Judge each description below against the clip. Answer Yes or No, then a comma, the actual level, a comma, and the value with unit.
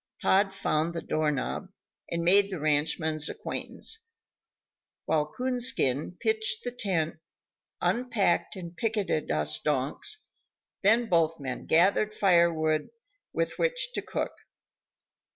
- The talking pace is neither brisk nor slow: No, slow, 115 wpm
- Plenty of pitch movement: Yes, wide, 6.5 semitones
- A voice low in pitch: No, medium, 175 Hz